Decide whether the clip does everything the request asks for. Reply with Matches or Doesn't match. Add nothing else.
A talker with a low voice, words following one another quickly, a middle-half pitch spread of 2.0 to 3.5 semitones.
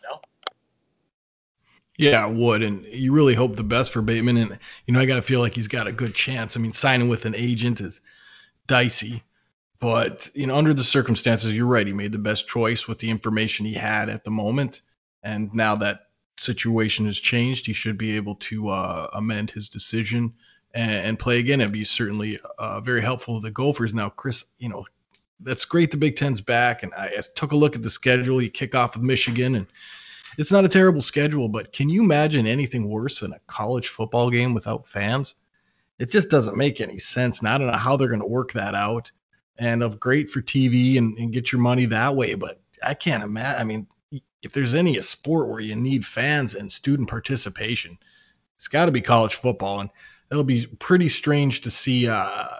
Matches